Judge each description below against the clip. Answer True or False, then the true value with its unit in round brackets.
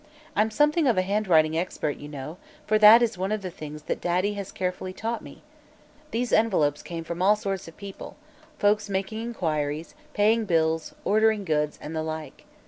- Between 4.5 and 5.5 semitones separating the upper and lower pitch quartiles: True (5.0 semitones)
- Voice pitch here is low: False (190 Hz)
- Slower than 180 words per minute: False (185 wpm)